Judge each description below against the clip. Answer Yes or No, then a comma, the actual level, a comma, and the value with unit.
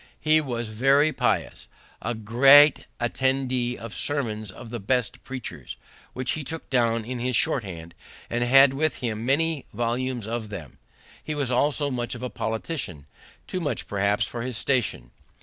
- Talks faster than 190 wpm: No, average, 165 wpm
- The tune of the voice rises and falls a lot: No, average, 3.5 semitones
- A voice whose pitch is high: No, low, 125 Hz